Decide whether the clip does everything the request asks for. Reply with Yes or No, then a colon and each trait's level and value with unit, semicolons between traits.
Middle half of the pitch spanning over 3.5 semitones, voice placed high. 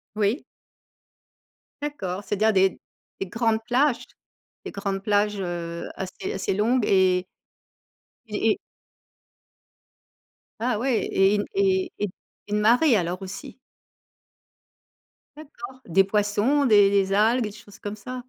Yes: average, 3.9 semitones; high, 210 Hz